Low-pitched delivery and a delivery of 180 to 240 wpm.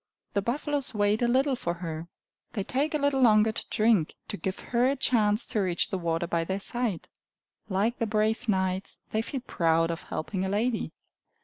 No: high, 210 Hz; average, 195 wpm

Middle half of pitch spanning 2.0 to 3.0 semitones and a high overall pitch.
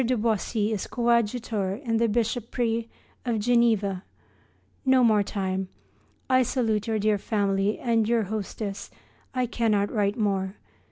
Yes: narrow, 2.6 semitones; high, 220 Hz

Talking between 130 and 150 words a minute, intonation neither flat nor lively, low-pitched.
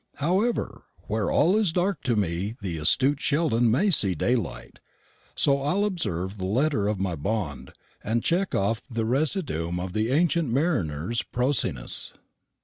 No: average, 145 wpm; wide, 8.4 semitones; low, 115 Hz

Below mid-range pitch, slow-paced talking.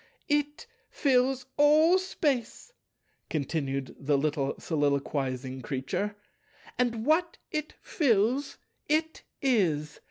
No: high, 230 Hz; slow, 90 wpm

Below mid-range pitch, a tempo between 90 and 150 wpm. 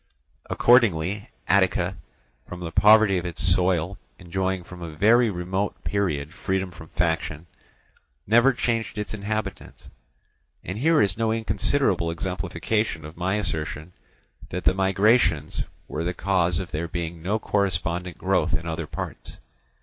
Yes: very low, 95 Hz; slow, 135 wpm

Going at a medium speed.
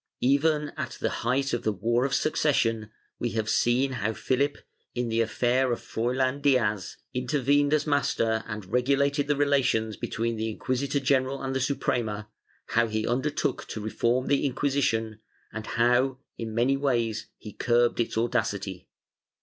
Yes: average, 155 wpm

